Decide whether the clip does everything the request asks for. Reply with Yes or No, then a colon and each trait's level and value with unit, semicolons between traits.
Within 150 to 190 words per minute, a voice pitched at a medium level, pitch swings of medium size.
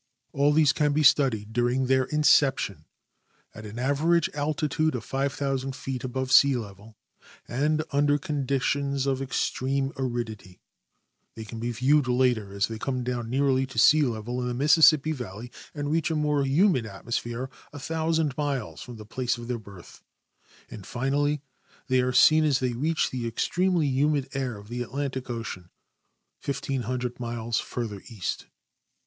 No: average, 155 wpm; low, 130 Hz; average, 3.4 semitones